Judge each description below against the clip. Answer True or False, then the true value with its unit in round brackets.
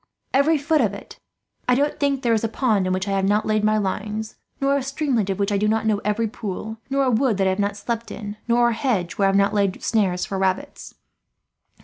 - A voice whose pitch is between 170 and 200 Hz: False (215 Hz)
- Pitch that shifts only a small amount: False (3.5 semitones)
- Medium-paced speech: False (260 wpm)